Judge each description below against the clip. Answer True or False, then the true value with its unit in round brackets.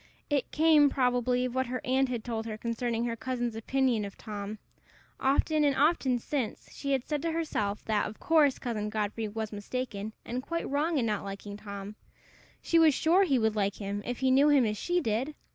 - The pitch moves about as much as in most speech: True (4.6 semitones)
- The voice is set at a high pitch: True (245 Hz)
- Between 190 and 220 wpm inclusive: True (205 wpm)